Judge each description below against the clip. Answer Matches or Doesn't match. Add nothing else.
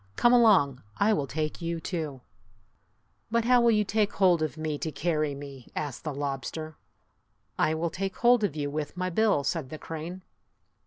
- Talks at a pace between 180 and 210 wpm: Matches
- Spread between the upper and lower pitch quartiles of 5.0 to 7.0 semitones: Matches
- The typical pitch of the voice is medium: Matches